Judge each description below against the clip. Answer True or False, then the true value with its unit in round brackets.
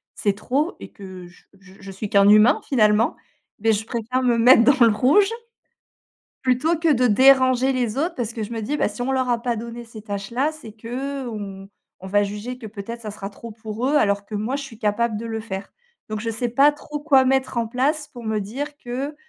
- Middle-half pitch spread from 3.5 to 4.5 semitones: True (3.8 semitones)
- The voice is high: True (235 Hz)